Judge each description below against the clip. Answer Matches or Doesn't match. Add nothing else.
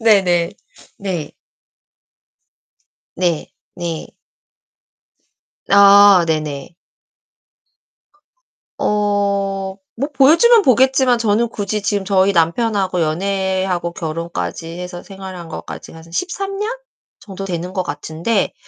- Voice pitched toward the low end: Doesn't match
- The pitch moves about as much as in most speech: Matches